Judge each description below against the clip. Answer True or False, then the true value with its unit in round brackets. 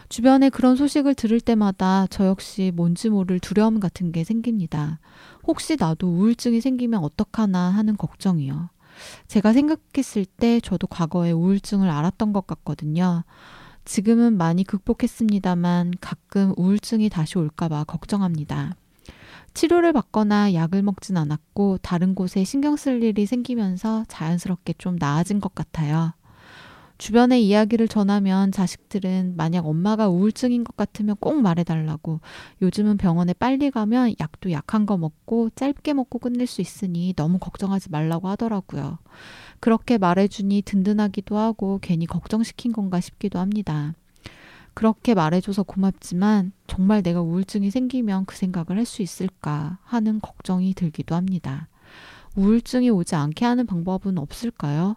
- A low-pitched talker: False (195 Hz)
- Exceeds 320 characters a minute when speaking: True (330 characters per minute)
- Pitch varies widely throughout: False (4.2 semitones)